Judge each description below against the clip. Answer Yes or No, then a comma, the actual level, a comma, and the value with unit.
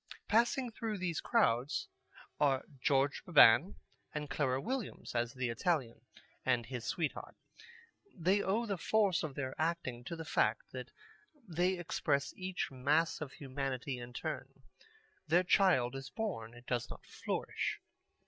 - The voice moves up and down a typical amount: No, wide, 6.1 semitones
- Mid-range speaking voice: Yes, medium, 145 Hz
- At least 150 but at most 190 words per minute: No, average, 140 wpm